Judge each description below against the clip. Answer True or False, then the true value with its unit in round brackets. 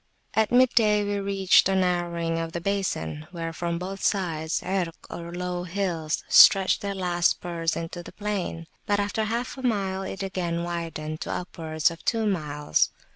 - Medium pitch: True (180 Hz)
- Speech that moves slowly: False (175 wpm)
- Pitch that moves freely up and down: False (3.0 semitones)